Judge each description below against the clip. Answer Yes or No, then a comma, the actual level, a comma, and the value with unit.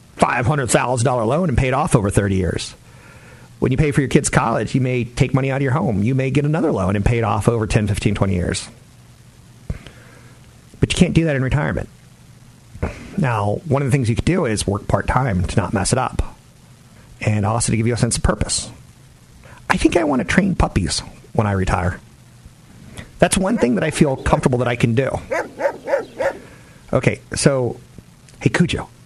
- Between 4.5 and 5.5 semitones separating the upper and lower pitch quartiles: Yes, average, 4.9 semitones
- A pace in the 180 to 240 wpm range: Yes, average, 195 wpm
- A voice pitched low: Yes, low, 125 Hz